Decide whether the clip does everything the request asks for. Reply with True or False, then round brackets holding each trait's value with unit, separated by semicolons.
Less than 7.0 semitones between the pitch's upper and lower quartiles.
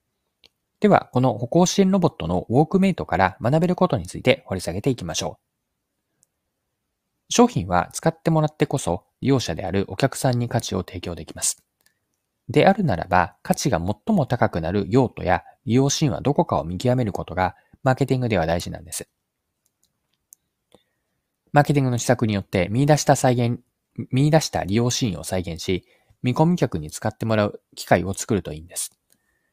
False (7.8 semitones)